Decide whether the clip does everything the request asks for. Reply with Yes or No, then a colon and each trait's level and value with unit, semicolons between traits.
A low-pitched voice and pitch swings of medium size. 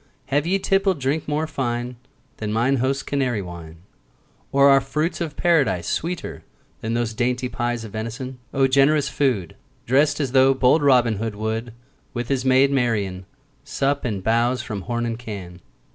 Yes: low, 125 Hz; average, 3.6 semitones